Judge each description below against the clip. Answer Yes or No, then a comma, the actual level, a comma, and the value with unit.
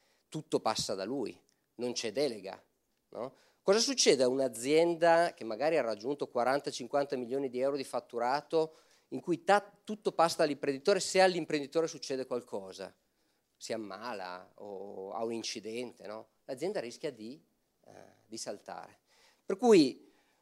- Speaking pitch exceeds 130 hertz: Yes, medium, 140 Hz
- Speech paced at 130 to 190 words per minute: Yes, average, 140 wpm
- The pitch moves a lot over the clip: Yes, wide, 5.7 semitones